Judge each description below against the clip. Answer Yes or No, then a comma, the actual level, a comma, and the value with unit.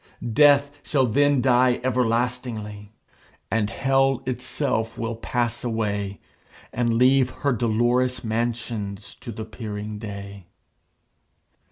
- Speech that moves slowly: Yes, slow, 100 wpm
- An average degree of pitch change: Yes, average, 3.0 semitones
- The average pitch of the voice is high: No, low, 120 Hz